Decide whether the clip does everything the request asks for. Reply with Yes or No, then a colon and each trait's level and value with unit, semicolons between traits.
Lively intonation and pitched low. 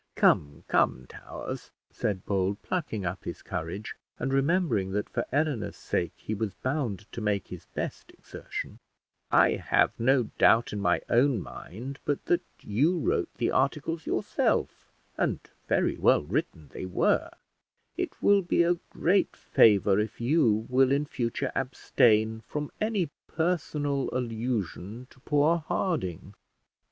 Yes: wide, 6.3 semitones; low, 125 Hz